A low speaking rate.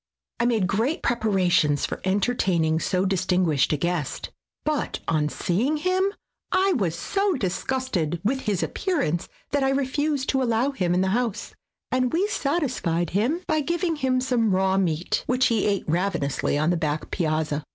No: average, 165 wpm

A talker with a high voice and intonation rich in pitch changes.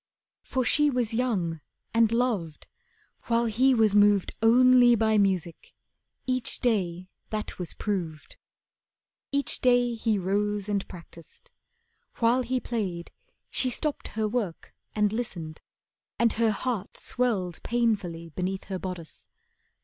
No: high, 215 Hz; average, 4.6 semitones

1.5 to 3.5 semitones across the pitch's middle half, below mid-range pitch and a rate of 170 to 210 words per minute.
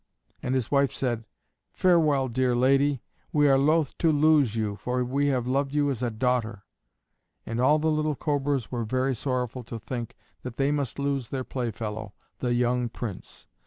Yes: average, 2.9 semitones; low, 130 Hz; average, 175 wpm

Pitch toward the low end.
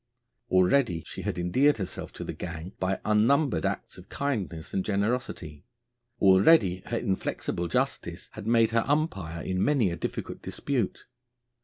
Yes: very low, 95 Hz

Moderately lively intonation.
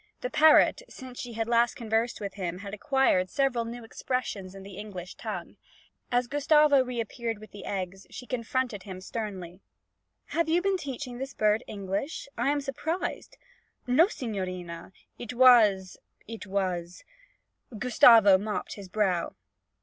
Yes: average, 4.7 semitones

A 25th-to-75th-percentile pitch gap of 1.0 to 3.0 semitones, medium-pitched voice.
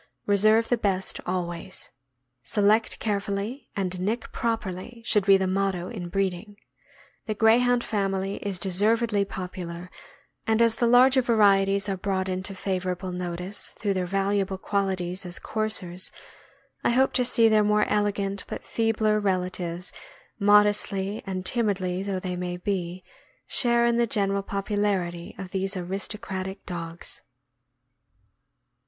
No: narrow, 2.6 semitones; high, 195 Hz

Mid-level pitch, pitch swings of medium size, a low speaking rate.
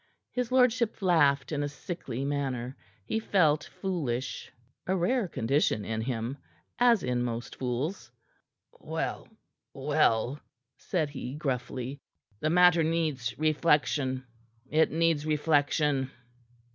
Yes: medium, 145 Hz; average, 4.6 semitones; slow, 110 wpm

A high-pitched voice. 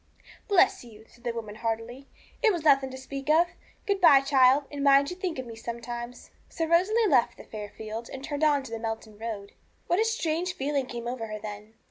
Yes: very high, 265 Hz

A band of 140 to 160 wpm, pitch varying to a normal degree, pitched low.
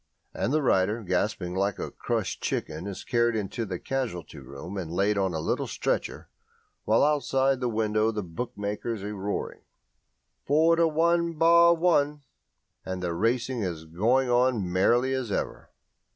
No: average, 155 wpm; wide, 5.8 semitones; low, 110 Hz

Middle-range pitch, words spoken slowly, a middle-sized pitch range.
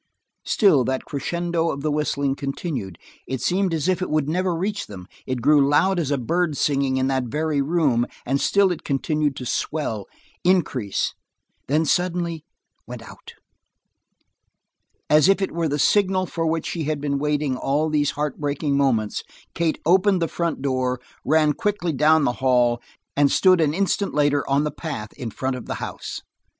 No: medium, 150 Hz; average, 175 wpm; average, 3.8 semitones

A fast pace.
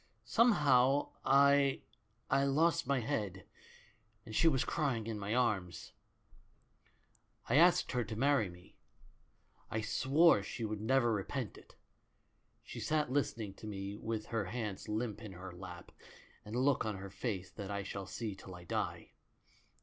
No: average, 155 wpm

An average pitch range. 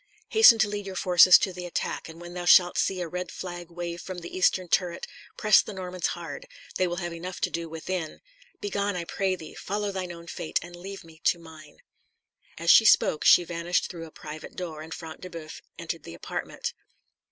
No: narrow, 1.8 semitones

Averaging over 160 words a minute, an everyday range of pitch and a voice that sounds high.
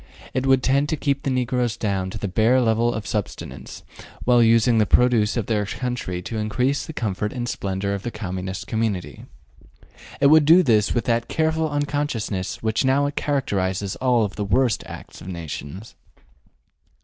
No: average, 170 wpm; average, 4.6 semitones; low, 115 Hz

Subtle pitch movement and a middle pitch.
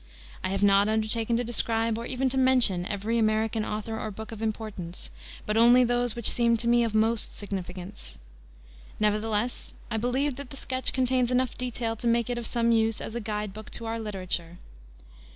No: narrow, 2.2 semitones; high, 225 Hz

